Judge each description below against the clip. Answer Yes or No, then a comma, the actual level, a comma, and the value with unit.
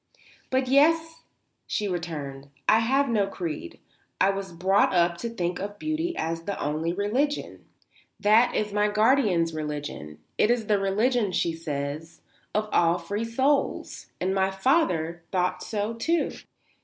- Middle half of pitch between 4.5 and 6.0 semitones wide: Yes, wide, 5.5 semitones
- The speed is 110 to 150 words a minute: Yes, average, 145 wpm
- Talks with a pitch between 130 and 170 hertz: No, high, 195 Hz